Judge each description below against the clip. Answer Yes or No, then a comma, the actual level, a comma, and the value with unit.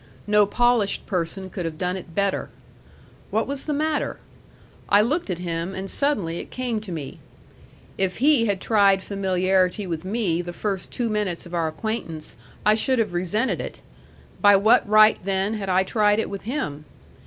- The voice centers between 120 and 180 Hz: No, high, 200 Hz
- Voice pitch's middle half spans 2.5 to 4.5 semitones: Yes, average, 3.4 semitones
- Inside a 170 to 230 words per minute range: Yes, average, 175 wpm